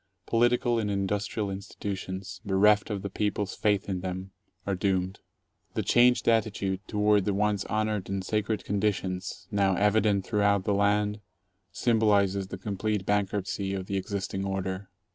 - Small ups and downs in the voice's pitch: Yes, narrow, 1.5 semitones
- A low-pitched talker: Yes, low, 100 Hz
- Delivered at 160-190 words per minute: No, average, 145 wpm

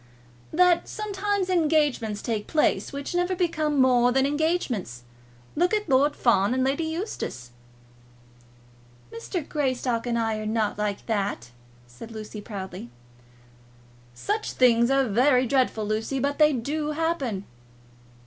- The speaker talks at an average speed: No, slow, 130 wpm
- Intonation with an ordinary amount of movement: No, wide, 6.2 semitones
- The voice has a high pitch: Yes, very high, 260 Hz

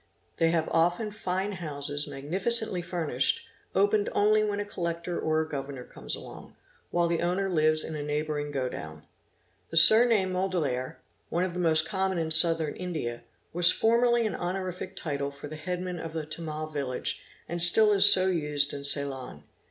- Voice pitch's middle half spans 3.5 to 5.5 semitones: Yes, average, 4.1 semitones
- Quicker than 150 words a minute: Yes, average, 170 wpm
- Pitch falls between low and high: Yes, medium, 165 Hz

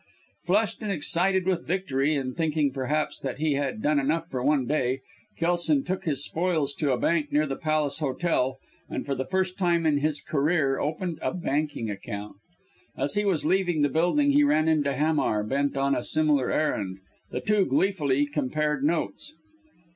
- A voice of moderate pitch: Yes, medium, 150 Hz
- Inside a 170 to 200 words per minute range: Yes, average, 175 wpm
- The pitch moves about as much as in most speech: Yes, average, 3.9 semitones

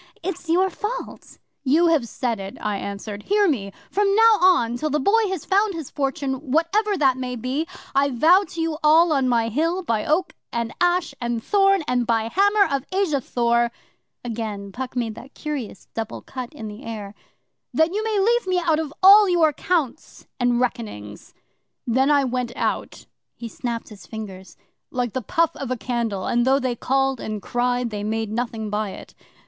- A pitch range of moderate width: No, wide, 6.6 semitones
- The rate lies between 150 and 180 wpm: No, average, 190 wpm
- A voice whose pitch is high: Yes, very high, 265 Hz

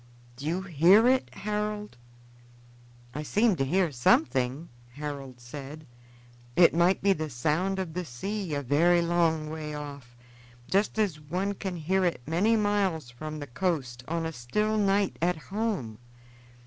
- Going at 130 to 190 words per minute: Yes, average, 150 wpm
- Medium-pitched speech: Yes, medium, 165 Hz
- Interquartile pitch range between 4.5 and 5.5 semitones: Yes, average, 5.2 semitones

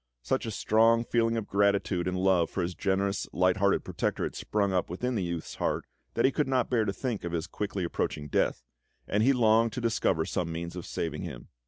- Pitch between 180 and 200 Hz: No, low, 100 Hz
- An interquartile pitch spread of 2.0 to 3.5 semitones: No, average, 4.2 semitones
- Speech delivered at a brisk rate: Yes, fast, 220 wpm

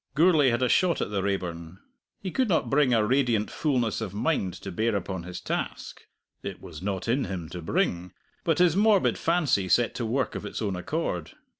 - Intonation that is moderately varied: No, wide, 8.0 semitones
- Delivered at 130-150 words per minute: No, average, 200 wpm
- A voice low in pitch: Yes, low, 115 Hz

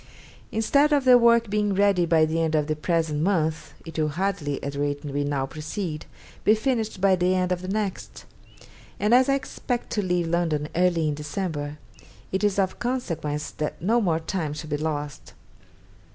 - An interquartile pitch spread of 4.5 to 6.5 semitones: Yes, average, 5.1 semitones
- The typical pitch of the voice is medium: Yes, medium, 170 Hz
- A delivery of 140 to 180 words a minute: No, average, 190 wpm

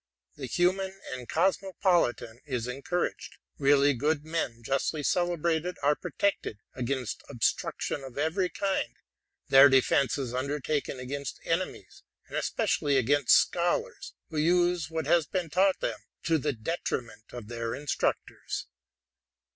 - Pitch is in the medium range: Yes, medium, 145 Hz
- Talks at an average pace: No, slow, 125 wpm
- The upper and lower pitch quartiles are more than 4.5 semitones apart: Yes, average, 5.1 semitones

